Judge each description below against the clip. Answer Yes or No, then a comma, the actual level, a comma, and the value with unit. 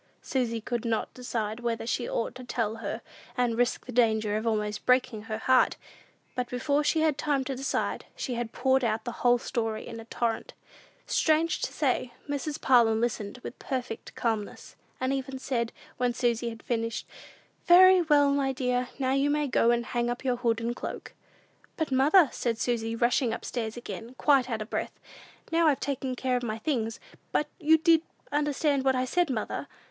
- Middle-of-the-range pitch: No, high, 245 Hz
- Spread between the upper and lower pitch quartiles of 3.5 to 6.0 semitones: No, average, 3.0 semitones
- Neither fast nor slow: Yes, average, 190 wpm